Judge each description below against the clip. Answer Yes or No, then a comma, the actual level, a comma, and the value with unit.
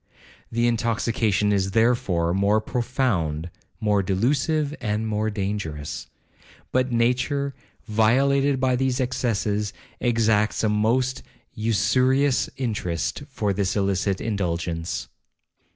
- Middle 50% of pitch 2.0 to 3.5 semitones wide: No, average, 4.1 semitones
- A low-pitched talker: Yes, low, 110 Hz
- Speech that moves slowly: Yes, slow, 100 wpm